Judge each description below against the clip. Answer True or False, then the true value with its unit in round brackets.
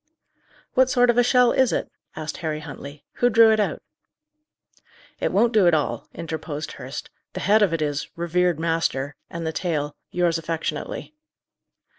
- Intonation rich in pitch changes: True (5.7 semitones)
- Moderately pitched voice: True (170 Hz)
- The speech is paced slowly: False (165 wpm)